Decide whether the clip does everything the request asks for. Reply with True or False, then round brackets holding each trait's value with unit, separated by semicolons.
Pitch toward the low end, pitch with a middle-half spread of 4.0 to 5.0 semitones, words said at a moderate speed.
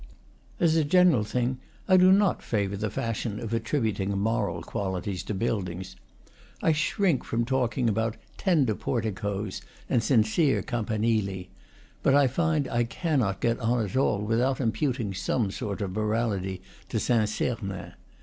True (115 Hz; 4.3 semitones; 145 wpm)